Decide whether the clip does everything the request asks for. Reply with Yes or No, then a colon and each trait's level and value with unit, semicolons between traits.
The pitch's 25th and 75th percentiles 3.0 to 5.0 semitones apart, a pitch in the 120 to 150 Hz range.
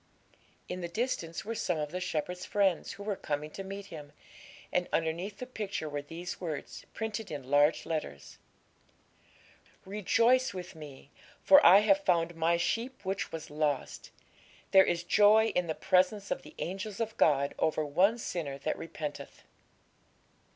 No: average, 4.5 semitones; medium, 180 Hz